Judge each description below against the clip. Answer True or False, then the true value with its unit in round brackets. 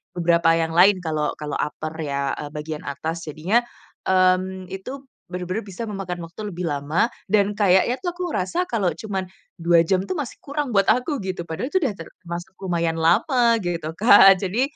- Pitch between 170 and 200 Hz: True (185 Hz)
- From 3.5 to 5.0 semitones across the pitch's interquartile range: True (4.2 semitones)